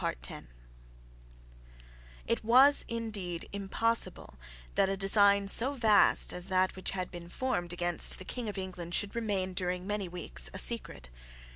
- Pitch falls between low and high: No, high, 195 Hz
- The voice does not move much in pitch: No, average, 3.7 semitones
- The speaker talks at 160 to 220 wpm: No, average, 140 wpm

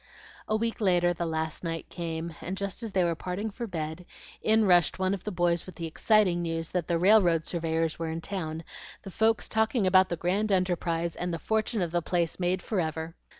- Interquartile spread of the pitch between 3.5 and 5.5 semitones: No, average, 3.1 semitones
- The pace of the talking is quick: Yes, fast, 210 wpm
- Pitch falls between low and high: Yes, medium, 175 Hz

